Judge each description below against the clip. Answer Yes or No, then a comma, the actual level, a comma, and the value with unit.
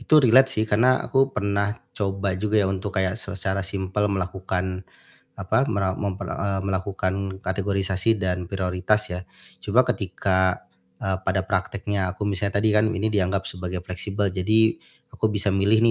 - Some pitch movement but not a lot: No, narrow, 2.0 semitones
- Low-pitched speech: Yes, low, 100 Hz